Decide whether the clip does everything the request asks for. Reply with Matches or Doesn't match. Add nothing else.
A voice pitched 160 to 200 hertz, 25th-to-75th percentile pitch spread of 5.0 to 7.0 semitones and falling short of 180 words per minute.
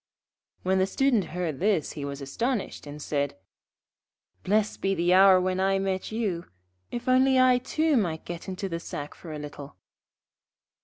Matches